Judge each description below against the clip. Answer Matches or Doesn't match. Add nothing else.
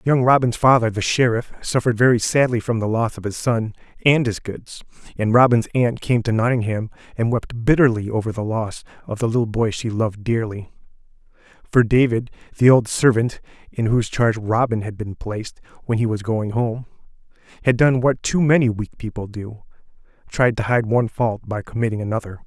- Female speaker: Doesn't match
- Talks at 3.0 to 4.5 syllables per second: Doesn't match